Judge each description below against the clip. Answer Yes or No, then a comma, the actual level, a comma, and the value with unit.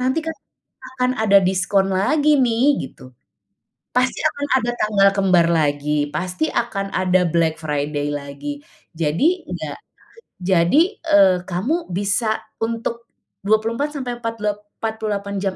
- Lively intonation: Yes, wide, 5.7 semitones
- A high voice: Yes, high, 200 Hz